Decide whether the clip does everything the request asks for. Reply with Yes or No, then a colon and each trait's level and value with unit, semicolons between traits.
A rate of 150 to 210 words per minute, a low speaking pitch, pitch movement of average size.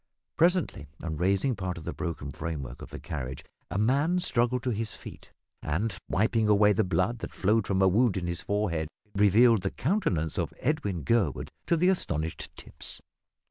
No: average, 180 wpm; low, 100 Hz; wide, 6.0 semitones